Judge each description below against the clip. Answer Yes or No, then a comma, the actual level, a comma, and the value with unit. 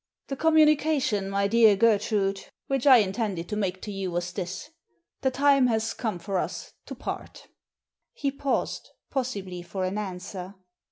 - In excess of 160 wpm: No, average, 155 wpm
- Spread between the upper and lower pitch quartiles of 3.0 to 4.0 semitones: No, wide, 5.4 semitones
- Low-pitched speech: No, high, 210 Hz